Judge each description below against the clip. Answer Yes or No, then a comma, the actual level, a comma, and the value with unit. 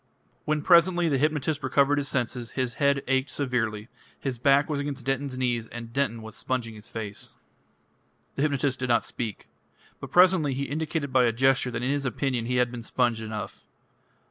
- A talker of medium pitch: No, low, 130 Hz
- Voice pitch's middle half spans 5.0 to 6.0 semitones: No, average, 3.1 semitones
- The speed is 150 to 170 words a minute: No, average, 185 wpm